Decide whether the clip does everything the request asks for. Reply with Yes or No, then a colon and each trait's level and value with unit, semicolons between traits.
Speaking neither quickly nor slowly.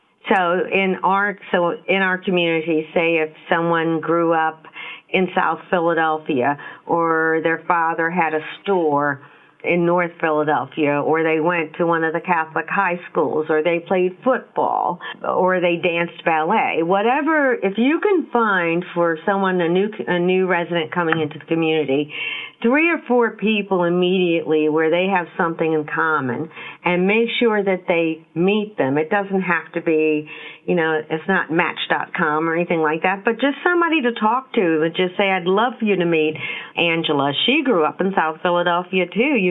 Yes: average, 175 wpm